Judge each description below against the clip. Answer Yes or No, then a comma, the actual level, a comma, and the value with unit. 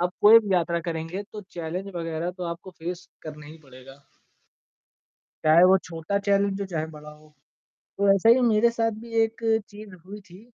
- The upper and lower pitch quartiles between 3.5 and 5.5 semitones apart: Yes, average, 3.9 semitones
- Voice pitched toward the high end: No, medium, 180 Hz